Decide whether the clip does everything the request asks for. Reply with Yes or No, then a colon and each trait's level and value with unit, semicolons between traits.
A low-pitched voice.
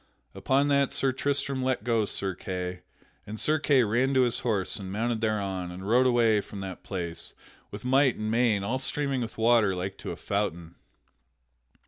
Yes: low, 115 Hz